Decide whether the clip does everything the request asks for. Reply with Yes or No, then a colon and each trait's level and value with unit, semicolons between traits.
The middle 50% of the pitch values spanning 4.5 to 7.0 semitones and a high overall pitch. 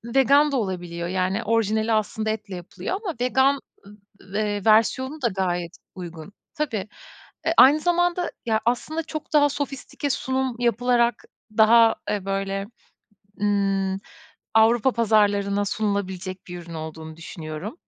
Yes: wide, 5.4 semitones; high, 215 Hz